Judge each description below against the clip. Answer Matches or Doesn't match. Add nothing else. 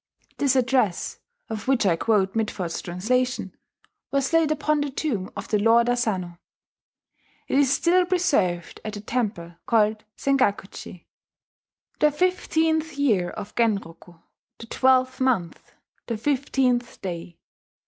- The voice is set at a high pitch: Matches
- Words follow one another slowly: Matches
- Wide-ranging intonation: Matches